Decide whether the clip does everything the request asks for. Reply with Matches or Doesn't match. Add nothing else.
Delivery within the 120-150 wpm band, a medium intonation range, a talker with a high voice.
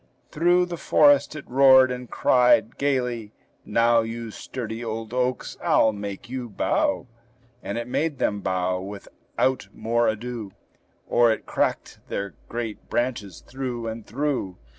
Doesn't match